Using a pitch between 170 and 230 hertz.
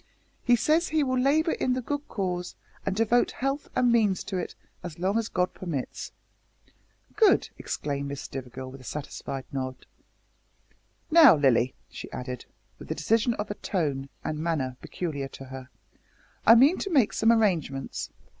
Yes: medium, 185 Hz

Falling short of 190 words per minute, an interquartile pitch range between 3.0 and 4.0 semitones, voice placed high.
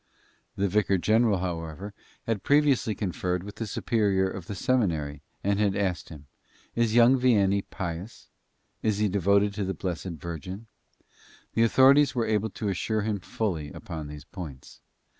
No: average, 155 wpm; average, 3.7 semitones; low, 100 Hz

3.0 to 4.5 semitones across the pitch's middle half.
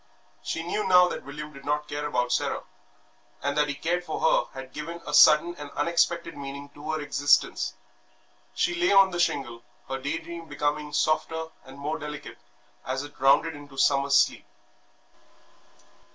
No: narrow, 2.5 semitones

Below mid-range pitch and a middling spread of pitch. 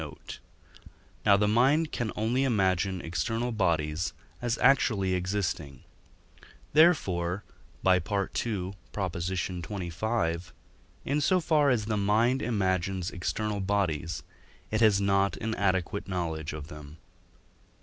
Yes: low, 100 Hz; average, 4.2 semitones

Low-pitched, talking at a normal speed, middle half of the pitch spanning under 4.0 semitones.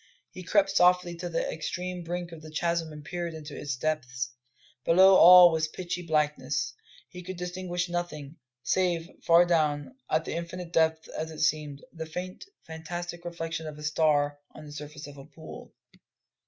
No: medium, 165 Hz; average, 170 wpm; narrow, 2.5 semitones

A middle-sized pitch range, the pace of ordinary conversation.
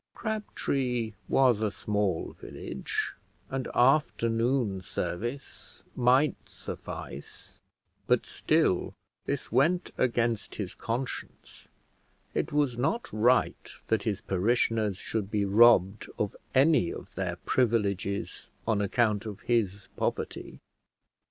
No: average, 4.0 semitones; slow, 105 wpm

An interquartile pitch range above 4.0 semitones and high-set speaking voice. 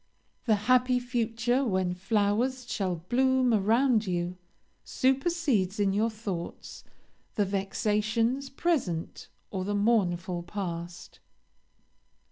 Yes: average, 4.8 semitones; high, 215 Hz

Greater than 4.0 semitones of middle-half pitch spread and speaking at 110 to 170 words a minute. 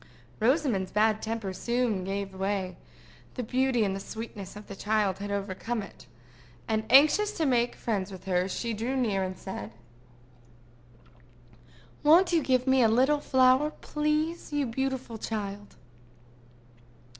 Yes: average, 5.0 semitones; slow, 135 wpm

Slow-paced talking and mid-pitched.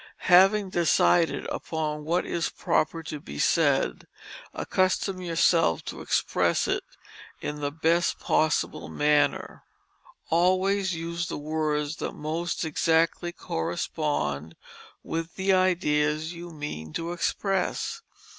Yes: slow, 110 wpm; medium, 165 Hz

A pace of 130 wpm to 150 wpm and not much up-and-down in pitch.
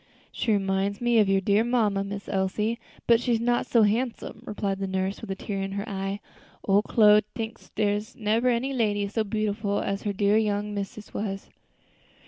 No: average, 185 wpm; narrow, 2.1 semitones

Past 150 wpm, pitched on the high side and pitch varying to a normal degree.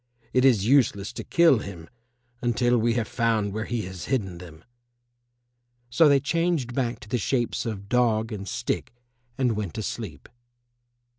No: average, 160 wpm; low, 115 Hz; average, 3.8 semitones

